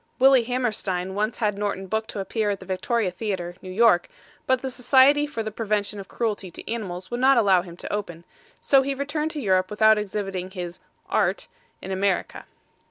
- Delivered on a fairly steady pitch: No, average, 4.3 semitones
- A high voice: Yes, high, 210 Hz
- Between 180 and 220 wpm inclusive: Yes, average, 195 wpm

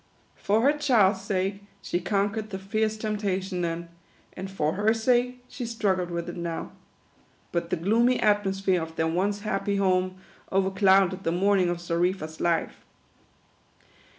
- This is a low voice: No, high, 195 Hz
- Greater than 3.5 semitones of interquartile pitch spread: No, average, 3.1 semitones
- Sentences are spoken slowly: No, average, 150 wpm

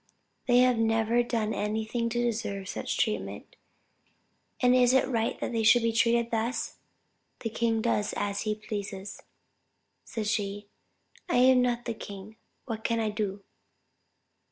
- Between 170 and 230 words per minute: No, average, 145 wpm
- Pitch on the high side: Yes, high, 225 Hz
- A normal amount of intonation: No, narrow, 2.1 semitones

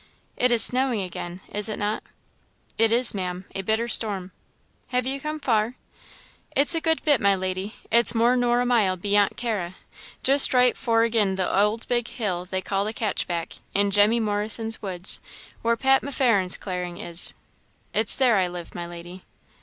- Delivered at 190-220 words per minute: No, average, 170 wpm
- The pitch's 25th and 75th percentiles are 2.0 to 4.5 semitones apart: Yes, average, 4.2 semitones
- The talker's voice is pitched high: Yes, high, 215 Hz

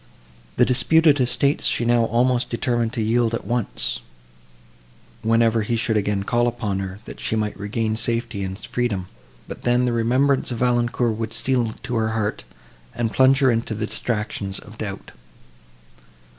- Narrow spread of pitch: Yes, narrow, 2.0 semitones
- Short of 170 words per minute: Yes, average, 160 wpm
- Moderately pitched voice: No, low, 115 Hz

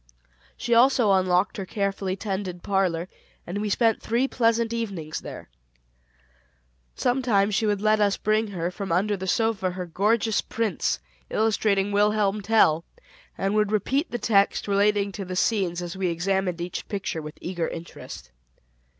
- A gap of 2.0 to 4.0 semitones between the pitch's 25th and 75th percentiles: Yes, average, 2.9 semitones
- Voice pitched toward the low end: No, high, 200 Hz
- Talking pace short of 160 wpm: Yes, average, 150 wpm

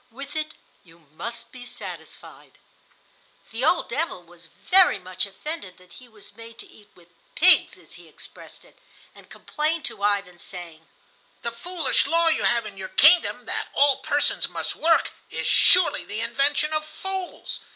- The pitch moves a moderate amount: No, wide, 8.5 semitones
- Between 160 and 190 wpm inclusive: Yes, average, 165 wpm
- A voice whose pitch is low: No, high, 235 Hz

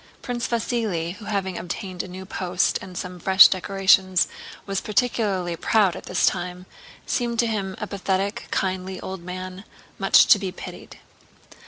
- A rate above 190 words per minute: No, average, 155 wpm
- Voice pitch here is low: No, high, 190 Hz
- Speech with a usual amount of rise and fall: No, narrow, 2.2 semitones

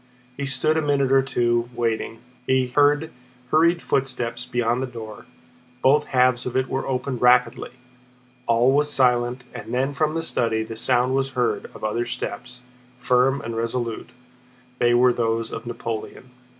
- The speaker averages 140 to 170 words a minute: Yes, average, 155 wpm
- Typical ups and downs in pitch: No, narrow, 2.1 semitones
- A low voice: Yes, low, 125 Hz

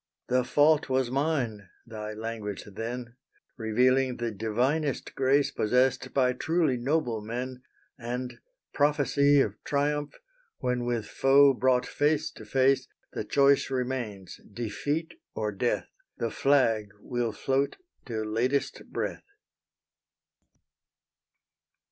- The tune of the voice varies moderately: Yes, average, 3.7 semitones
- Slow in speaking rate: Yes, slow, 110 wpm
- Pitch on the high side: No, low, 125 Hz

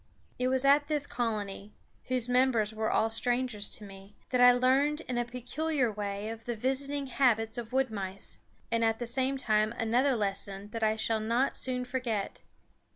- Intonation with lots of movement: No, average, 3.1 semitones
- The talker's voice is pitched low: No, high, 240 Hz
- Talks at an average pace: Yes, average, 180 wpm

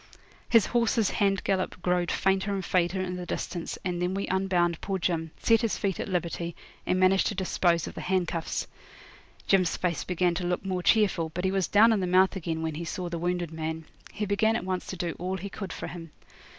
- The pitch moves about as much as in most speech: No, narrow, 2.0 semitones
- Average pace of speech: No, fast, 220 wpm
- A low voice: No, medium, 185 Hz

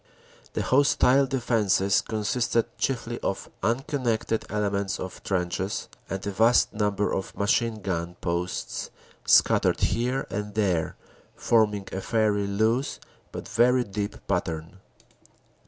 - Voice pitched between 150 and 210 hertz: No, low, 105 Hz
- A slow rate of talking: Yes, slow, 120 wpm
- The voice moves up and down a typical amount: Yes, average, 3.4 semitones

